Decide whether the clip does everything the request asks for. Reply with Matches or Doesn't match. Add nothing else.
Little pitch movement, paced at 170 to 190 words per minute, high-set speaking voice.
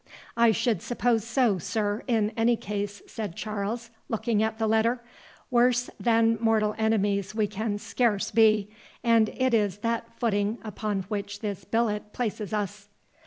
Doesn't match